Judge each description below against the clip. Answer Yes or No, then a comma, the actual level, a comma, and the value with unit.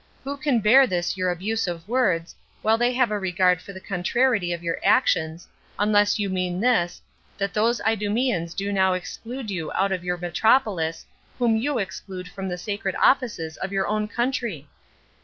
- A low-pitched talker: No, high, 200 Hz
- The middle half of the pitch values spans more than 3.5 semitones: Yes, average, 4.1 semitones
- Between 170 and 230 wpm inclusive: Yes, average, 175 wpm